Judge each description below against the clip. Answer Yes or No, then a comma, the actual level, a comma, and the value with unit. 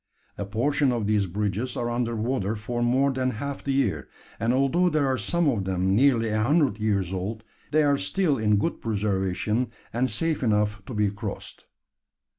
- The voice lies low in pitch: Yes, low, 115 Hz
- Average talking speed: Yes, average, 185 wpm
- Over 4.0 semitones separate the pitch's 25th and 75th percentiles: Yes, average, 4.5 semitones